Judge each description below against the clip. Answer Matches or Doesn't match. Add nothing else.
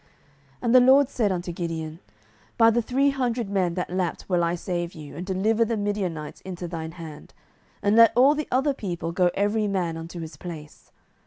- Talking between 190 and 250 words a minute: Matches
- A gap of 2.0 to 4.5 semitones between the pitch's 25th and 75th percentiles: Doesn't match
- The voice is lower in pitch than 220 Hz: Matches